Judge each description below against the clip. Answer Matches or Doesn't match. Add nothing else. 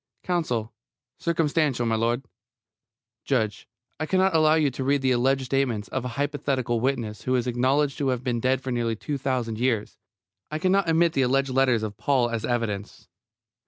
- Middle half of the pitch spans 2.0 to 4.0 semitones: Matches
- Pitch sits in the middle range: Doesn't match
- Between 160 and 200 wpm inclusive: Matches